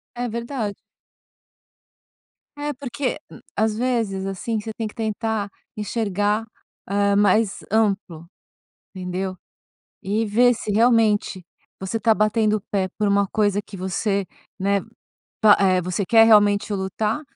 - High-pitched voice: Yes, high, 210 Hz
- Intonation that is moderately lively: No, narrow, 2.2 semitones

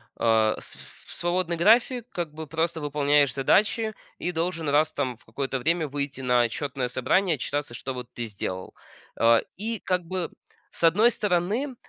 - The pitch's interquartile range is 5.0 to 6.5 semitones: Yes, wide, 5.5 semitones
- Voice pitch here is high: No, medium, 155 Hz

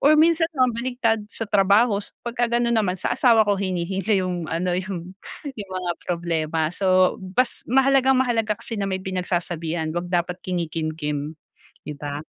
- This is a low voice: No, high, 190 Hz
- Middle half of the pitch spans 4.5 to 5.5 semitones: Yes, average, 5.1 semitones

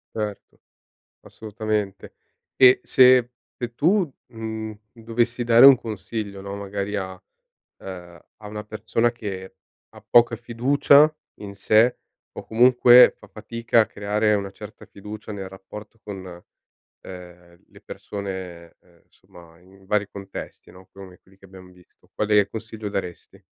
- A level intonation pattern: No, average, 3.1 semitones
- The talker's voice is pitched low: Yes, low, 105 Hz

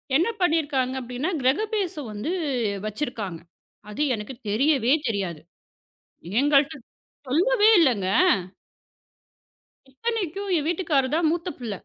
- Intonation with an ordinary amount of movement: No, wide, 5.9 semitones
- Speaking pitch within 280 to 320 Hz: Yes, very high, 285 Hz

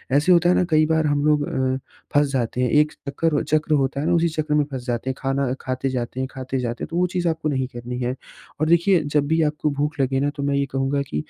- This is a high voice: No, medium, 145 Hz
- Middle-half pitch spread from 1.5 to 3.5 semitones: Yes, average, 2.8 semitones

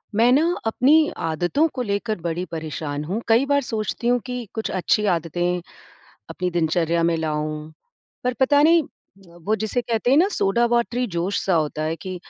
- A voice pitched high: Yes, high, 200 Hz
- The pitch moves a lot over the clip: Yes, wide, 6.9 semitones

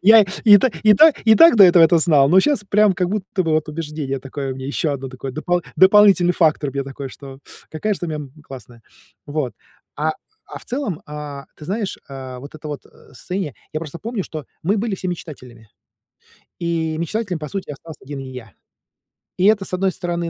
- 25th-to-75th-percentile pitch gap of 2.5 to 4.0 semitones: No, wide, 5.4 semitones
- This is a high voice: No, medium, 160 Hz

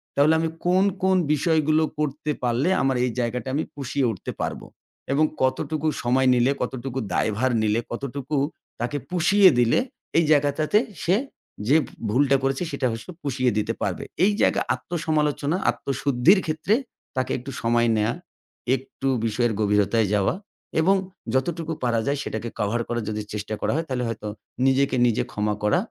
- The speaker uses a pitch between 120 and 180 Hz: Yes, low, 135 Hz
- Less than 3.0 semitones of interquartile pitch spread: No, average, 4.4 semitones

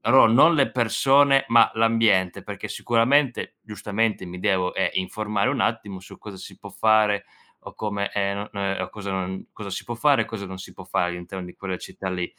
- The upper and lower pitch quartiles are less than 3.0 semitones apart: No, average, 3.3 semitones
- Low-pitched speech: Yes, low, 105 Hz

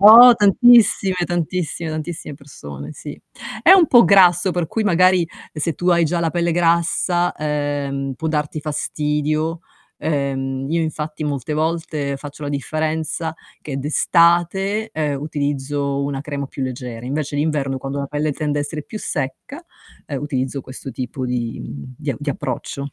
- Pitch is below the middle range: No, medium, 150 Hz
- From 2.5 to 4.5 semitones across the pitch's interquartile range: Yes, average, 3.5 semitones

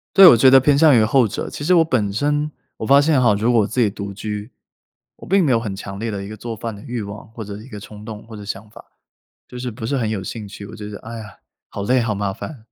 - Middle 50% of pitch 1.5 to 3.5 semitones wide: No, average, 3.9 semitones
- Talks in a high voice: No, low, 110 Hz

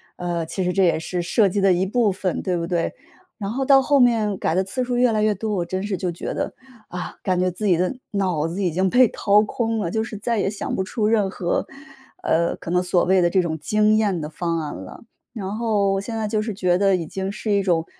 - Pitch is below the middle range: No, high, 195 Hz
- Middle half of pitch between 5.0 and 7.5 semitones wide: No, average, 3.3 semitones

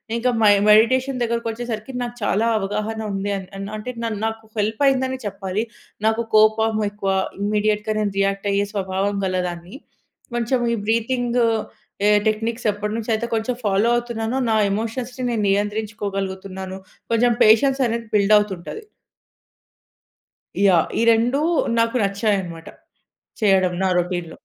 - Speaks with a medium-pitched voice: No, high, 215 Hz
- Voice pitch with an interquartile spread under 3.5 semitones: Yes, average, 2.8 semitones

